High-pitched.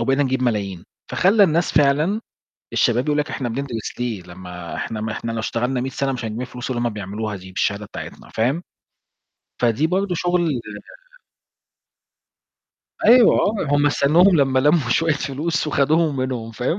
No: low, 130 Hz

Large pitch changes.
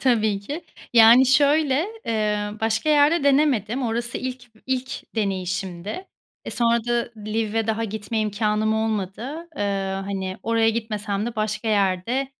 No: average, 3.4 semitones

